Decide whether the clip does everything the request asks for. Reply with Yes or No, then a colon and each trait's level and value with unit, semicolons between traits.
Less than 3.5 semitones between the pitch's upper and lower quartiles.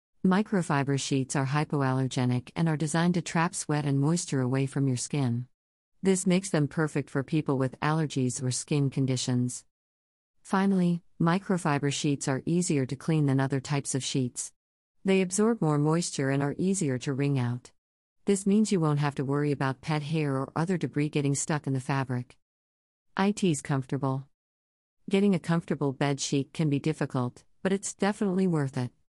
No: average, 3.9 semitones